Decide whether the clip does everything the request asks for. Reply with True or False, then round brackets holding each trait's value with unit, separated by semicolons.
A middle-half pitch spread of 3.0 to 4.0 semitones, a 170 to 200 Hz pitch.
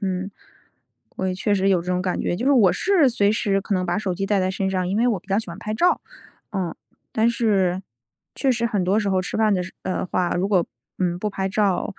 False (2.6 semitones; 195 Hz)